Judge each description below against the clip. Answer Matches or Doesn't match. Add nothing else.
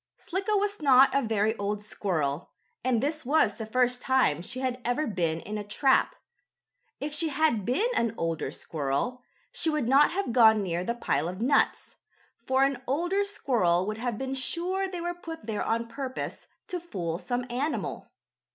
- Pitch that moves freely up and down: Matches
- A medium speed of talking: Matches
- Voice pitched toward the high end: Matches